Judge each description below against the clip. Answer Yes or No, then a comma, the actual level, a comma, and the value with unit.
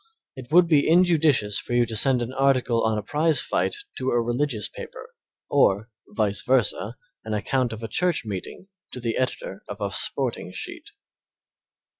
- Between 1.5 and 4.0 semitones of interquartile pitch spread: No, average, 4.6 semitones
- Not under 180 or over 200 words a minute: No, average, 170 wpm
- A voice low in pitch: Yes, low, 120 Hz